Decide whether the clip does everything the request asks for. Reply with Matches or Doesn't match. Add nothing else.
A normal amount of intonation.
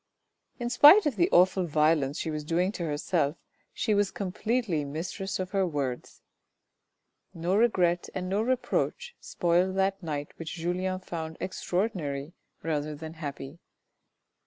Matches